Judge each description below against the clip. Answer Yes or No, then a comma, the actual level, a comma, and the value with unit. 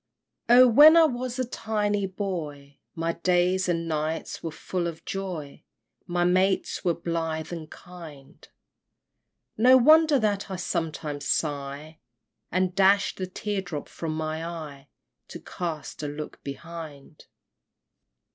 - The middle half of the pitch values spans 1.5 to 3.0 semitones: No, average, 3.9 semitones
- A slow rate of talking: Yes, slow, 130 wpm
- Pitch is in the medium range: Yes, medium, 170 Hz